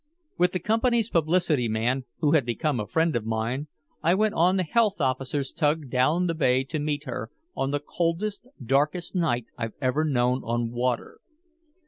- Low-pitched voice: No, medium, 145 Hz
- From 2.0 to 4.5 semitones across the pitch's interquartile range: No, average, 5.3 semitones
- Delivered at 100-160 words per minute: No, average, 175 wpm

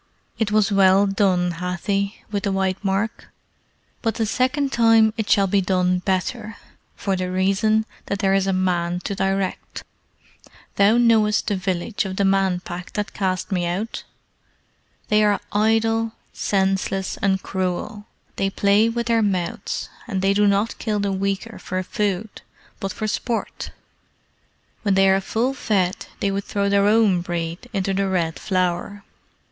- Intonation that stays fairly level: Yes, narrow, 2.2 semitones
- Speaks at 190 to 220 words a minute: No, average, 160 wpm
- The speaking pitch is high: Yes, high, 195 Hz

